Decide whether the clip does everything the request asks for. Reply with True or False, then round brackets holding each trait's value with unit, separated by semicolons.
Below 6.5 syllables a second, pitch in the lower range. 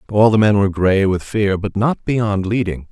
True (4.8 syllables/s; 100 Hz)